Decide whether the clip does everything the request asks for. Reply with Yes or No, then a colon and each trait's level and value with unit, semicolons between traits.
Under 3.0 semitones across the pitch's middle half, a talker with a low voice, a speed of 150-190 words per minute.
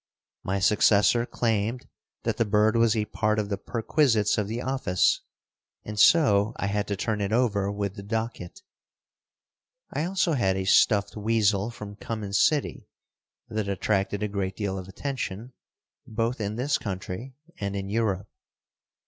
Yes: narrow, 2.5 semitones; low, 105 Hz; average, 155 wpm